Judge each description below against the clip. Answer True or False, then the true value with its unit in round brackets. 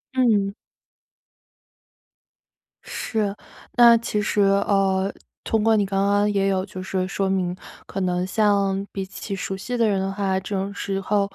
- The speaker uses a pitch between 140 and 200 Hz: True (195 Hz)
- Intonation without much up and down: True (1.3 semitones)